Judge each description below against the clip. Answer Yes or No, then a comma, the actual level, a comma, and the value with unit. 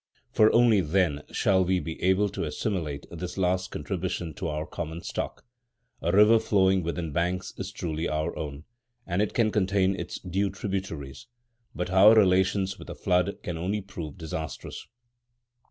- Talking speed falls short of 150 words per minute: No, average, 160 wpm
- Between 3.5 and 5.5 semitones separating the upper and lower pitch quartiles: No, average, 2.9 semitones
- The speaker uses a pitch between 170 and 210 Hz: No, very low, 90 Hz